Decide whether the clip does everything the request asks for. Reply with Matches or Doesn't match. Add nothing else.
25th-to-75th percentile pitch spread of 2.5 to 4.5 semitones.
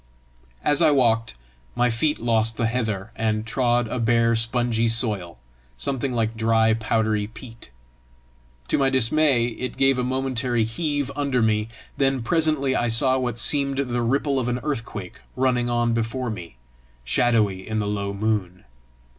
Matches